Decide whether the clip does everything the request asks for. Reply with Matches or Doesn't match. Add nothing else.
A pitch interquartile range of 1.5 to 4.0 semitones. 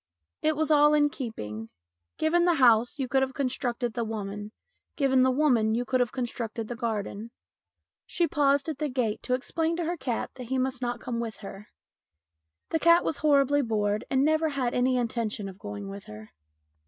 Doesn't match